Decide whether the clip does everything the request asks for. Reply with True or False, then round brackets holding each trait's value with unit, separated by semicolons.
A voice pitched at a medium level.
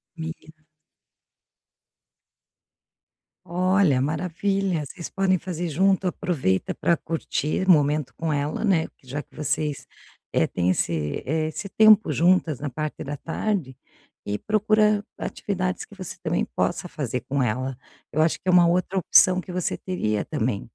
True (165 Hz)